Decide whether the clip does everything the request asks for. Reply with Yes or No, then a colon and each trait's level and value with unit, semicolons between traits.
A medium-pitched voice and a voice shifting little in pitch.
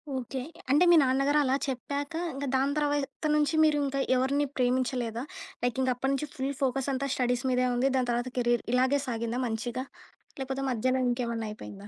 No: very high, 260 Hz; narrow, 2.1 semitones